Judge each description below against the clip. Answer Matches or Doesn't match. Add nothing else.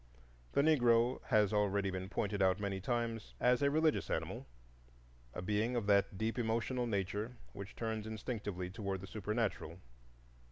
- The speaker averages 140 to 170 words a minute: Matches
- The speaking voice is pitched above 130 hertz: Doesn't match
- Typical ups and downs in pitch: Matches